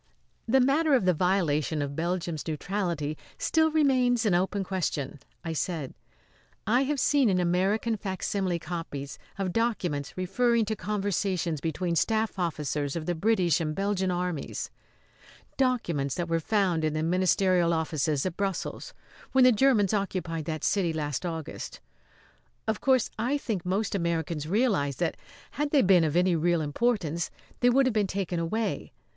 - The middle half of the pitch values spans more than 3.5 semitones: Yes, average, 5.0 semitones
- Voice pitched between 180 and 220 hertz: Yes, medium, 185 Hz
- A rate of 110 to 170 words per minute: Yes, average, 155 wpm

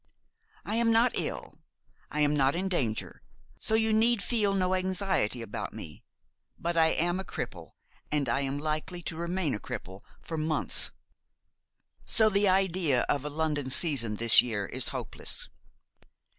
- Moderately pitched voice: Yes, medium, 160 Hz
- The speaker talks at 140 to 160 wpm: Yes, average, 155 wpm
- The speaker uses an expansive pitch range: Yes, wide, 5.9 semitones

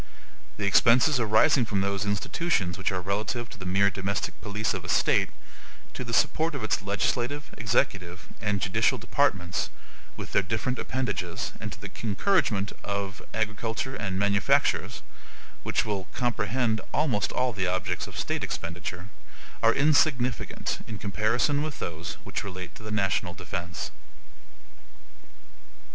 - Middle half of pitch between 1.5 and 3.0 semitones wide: No, average, 3.8 semitones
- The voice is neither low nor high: No, low, 105 Hz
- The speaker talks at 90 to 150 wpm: Yes, average, 140 wpm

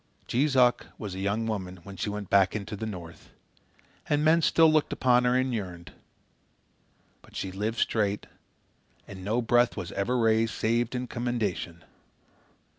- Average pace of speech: Yes, average, 160 wpm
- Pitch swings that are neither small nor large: Yes, average, 3.9 semitones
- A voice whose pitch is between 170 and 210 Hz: No, low, 110 Hz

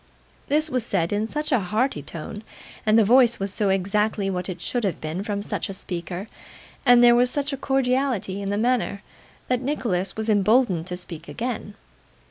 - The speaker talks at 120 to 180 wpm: No, average, 190 wpm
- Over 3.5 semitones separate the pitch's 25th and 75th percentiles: Yes, average, 4.6 semitones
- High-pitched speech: Yes, high, 210 Hz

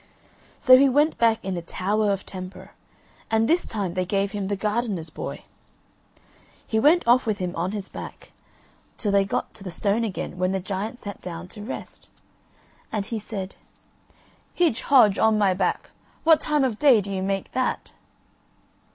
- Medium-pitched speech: No, high, 205 Hz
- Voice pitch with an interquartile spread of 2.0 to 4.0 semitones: Yes, average, 3.5 semitones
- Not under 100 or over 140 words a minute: No, average, 180 wpm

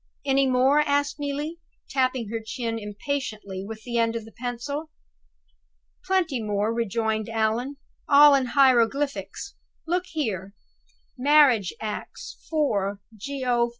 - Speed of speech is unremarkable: No, slow, 115 wpm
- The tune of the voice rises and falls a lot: No, average, 4.4 semitones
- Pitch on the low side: No, high, 245 Hz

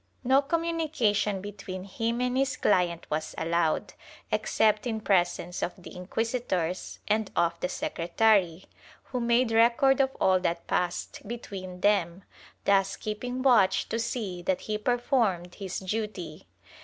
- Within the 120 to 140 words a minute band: Yes, slow, 135 wpm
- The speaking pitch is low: No, high, 205 Hz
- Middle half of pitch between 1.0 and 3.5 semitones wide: No, average, 4.7 semitones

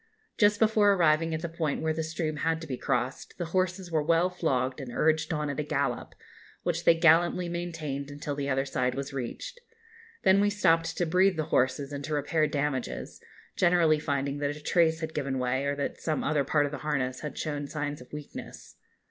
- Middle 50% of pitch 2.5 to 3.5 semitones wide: Yes, average, 2.9 semitones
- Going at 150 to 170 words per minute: No, fast, 205 wpm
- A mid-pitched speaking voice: Yes, medium, 155 Hz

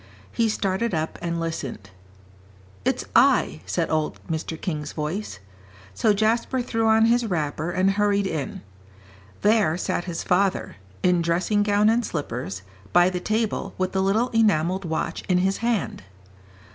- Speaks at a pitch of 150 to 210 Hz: Yes, medium, 185 Hz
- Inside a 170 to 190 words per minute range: No, average, 145 wpm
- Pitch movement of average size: Yes, average, 4.8 semitones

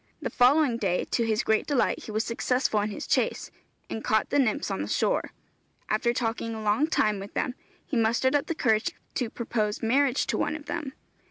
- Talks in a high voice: Yes, high, 230 Hz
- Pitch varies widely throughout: No, average, 3.4 semitones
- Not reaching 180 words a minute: No, fast, 205 wpm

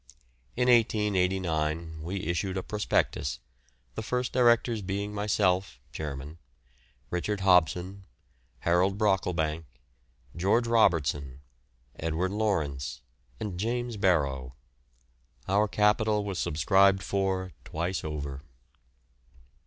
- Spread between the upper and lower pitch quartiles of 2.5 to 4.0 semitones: No, average, 4.6 semitones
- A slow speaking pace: Yes, slow, 90 wpm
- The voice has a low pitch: Yes, very low, 95 Hz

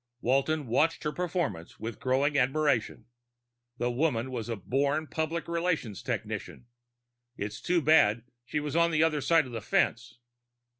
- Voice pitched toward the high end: No, medium, 140 Hz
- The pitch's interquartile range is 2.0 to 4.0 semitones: No, average, 5.1 semitones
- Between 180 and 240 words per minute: No, average, 155 wpm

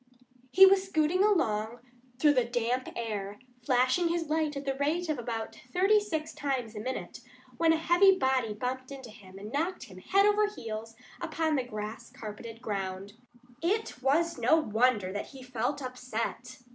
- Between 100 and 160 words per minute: No, average, 170 wpm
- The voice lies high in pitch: Yes, very high, 260 Hz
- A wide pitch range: Yes, wide, 6.3 semitones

